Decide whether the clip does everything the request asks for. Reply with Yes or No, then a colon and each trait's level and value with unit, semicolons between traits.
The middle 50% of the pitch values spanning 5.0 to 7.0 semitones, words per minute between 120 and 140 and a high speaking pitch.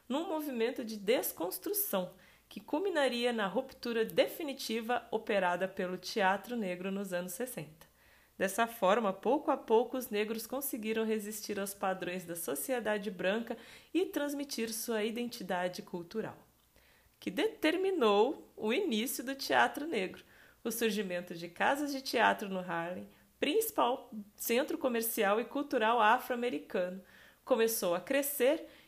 Yes: wide, 5.4 semitones; average, 125 wpm; high, 225 Hz